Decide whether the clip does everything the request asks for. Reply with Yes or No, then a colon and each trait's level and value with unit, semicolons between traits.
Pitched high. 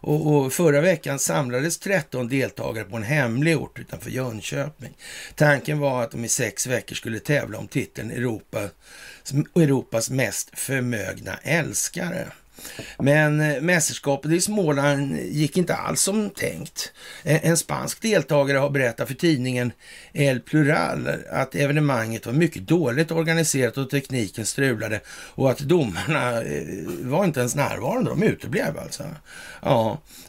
No: medium, 140 Hz